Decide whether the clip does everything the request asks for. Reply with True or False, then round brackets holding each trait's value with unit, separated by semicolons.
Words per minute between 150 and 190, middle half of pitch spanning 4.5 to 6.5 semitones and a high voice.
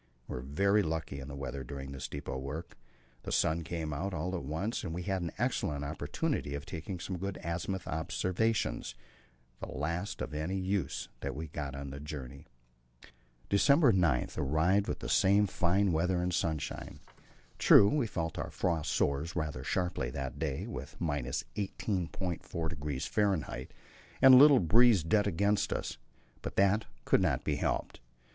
False (165 wpm; 5.1 semitones; 85 Hz)